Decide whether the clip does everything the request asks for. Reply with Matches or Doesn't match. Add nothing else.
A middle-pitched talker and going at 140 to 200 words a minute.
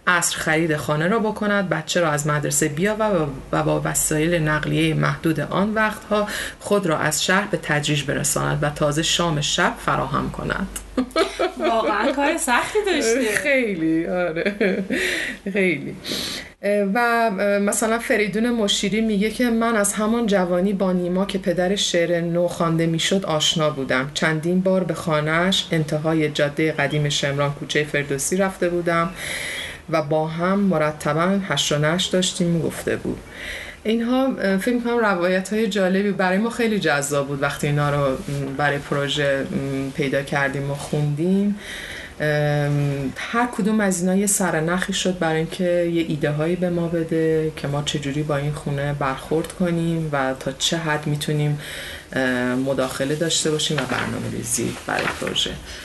Matches